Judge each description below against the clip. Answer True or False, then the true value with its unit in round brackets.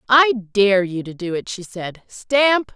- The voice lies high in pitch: True (215 Hz)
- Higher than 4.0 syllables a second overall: False (3.6 syllables/s)